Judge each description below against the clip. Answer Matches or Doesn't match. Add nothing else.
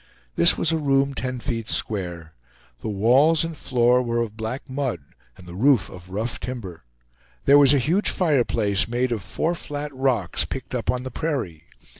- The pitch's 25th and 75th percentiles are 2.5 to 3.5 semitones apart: Doesn't match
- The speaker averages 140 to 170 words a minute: Doesn't match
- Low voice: Matches